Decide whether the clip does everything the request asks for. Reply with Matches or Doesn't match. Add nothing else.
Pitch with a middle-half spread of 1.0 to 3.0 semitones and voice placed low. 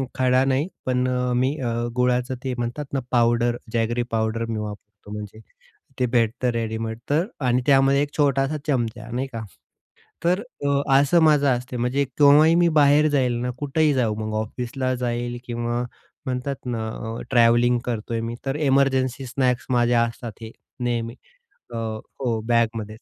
Matches